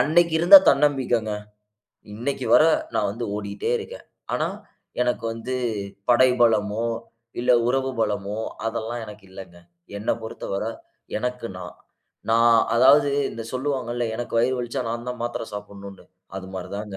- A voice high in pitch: No, low, 115 Hz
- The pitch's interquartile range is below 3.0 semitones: No, average, 3.5 semitones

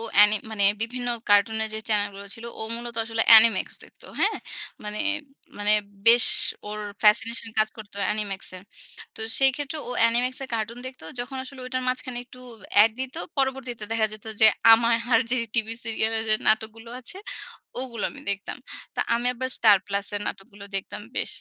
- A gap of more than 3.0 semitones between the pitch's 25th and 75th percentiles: No, average, 2.7 semitones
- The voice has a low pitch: No, high, 225 Hz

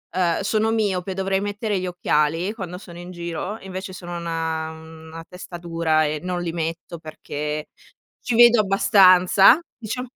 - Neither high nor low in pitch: Yes, medium, 180 Hz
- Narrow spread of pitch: No, average, 3.1 semitones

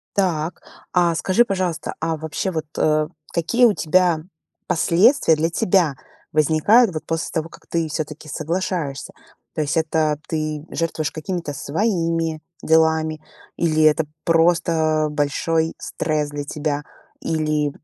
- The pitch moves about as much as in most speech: No, narrow, 1.7 semitones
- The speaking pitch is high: No, medium, 160 Hz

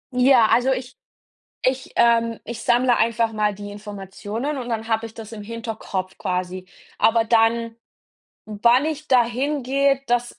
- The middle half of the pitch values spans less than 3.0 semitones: Yes, narrow, 2.6 semitones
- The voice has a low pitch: No, high, 230 Hz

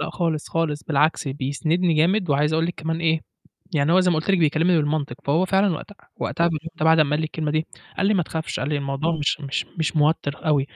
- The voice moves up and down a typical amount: No, narrow, 2.2 semitones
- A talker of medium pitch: Yes, medium, 160 Hz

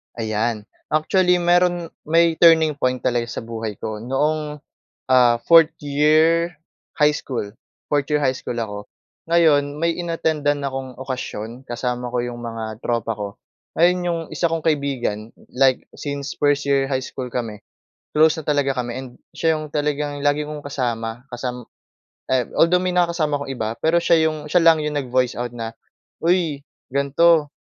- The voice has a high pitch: No, medium, 145 Hz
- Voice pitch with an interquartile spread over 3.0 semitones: Yes, average, 4.5 semitones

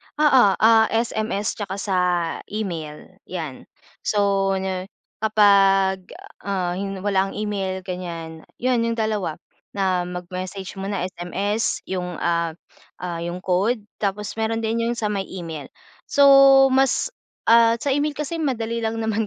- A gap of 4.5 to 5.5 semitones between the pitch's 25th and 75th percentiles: No, average, 3.3 semitones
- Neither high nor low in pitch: No, high, 195 Hz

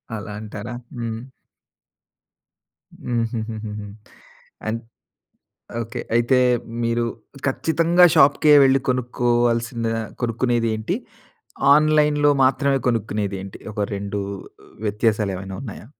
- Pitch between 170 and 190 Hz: No, low, 115 Hz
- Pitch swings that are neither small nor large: Yes, average, 3.2 semitones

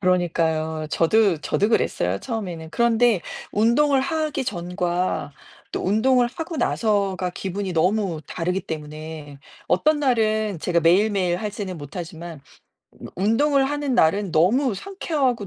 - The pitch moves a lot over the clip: Yes, wide, 5.9 semitones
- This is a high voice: Yes, high, 195 Hz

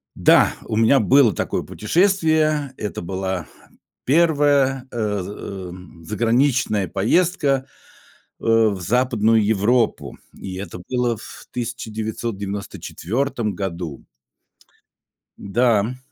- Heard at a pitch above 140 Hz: No, low, 115 Hz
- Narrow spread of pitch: No, average, 4.9 semitones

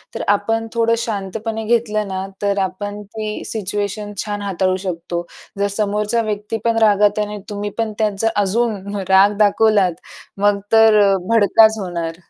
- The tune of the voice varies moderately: No, narrow, 1.7 semitones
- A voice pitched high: Yes, high, 210 Hz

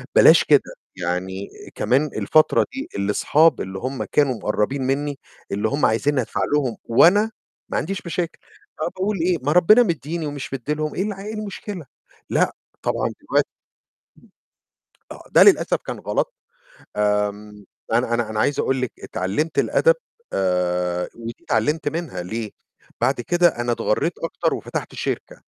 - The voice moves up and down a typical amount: No, wide, 7.8 semitones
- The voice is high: No, low, 135 Hz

